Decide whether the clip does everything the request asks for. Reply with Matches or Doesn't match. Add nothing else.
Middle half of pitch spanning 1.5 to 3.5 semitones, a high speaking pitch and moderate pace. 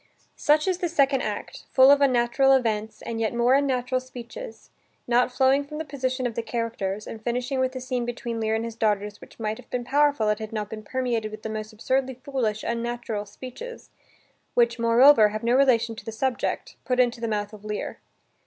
Doesn't match